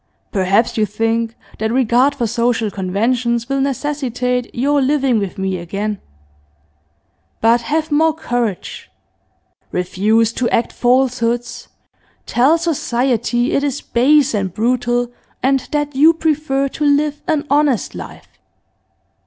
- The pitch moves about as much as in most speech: Yes, average, 3.9 semitones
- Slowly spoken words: Yes, slow, 120 wpm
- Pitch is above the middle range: Yes, high, 245 Hz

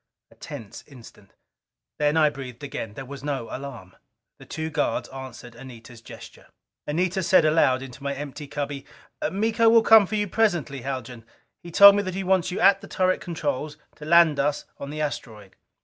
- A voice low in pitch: No, medium, 145 Hz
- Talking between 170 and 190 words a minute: Yes, average, 180 wpm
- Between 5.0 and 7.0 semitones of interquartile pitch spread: Yes, wide, 5.4 semitones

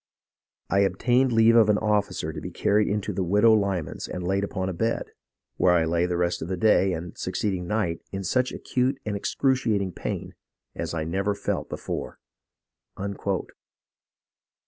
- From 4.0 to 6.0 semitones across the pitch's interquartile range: No, average, 3.5 semitones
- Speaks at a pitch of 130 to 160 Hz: No, low, 100 Hz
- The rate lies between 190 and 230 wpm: No, average, 165 wpm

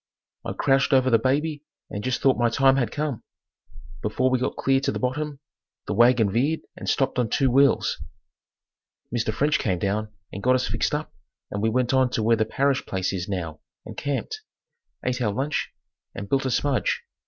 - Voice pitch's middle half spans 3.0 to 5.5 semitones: Yes, average, 3.6 semitones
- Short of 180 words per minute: No, average, 195 wpm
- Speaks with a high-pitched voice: No, low, 130 Hz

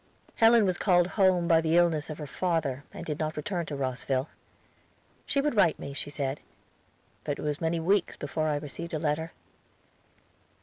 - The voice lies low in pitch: No, medium, 160 Hz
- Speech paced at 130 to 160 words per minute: No, average, 180 wpm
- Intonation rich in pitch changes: No, average, 3.1 semitones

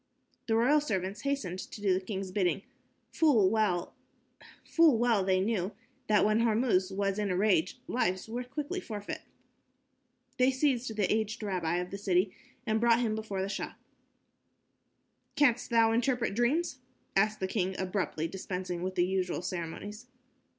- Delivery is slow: No, average, 150 wpm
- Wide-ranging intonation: No, average, 3.9 semitones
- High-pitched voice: Yes, high, 210 Hz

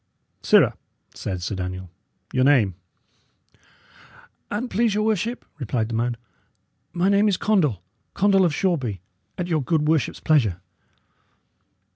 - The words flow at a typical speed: No, slow, 125 wpm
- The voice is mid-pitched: Yes, medium, 150 Hz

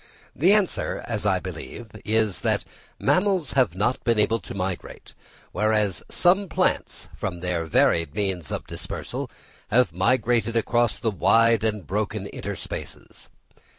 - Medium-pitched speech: No, low, 110 Hz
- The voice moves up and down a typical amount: Yes, average, 4.2 semitones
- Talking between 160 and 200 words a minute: No, slow, 135 wpm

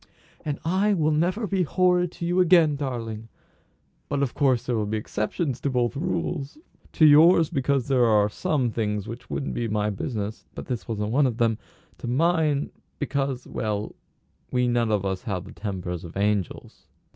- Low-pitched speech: Yes, low, 125 Hz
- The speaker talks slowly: No, average, 180 wpm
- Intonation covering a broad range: Yes, wide, 6.0 semitones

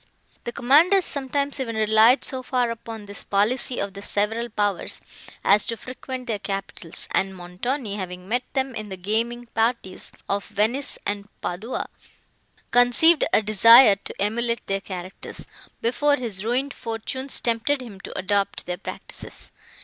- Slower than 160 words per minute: Yes, average, 150 wpm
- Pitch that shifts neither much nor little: Yes, average, 3.9 semitones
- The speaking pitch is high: Yes, high, 225 Hz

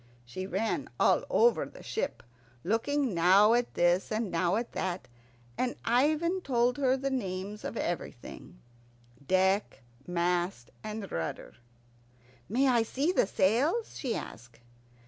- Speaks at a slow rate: Yes, slow, 130 wpm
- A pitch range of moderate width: No, wide, 6.2 semitones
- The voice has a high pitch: Yes, high, 215 Hz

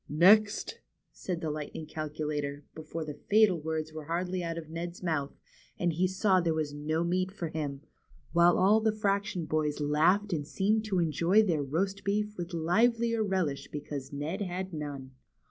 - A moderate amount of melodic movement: Yes, average, 4.0 semitones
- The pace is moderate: Yes, average, 175 wpm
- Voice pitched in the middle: Yes, medium, 170 Hz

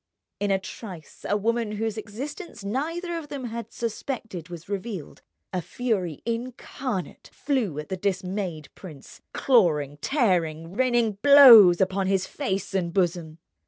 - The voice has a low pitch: No, high, 200 Hz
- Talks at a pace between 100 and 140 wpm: Yes, slow, 135 wpm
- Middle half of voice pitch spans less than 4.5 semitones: No, average, 5.0 semitones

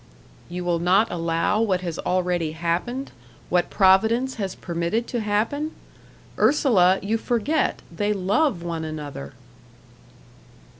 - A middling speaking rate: No, slow, 115 wpm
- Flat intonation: No, average, 4.8 semitones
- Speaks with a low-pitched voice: No, high, 190 Hz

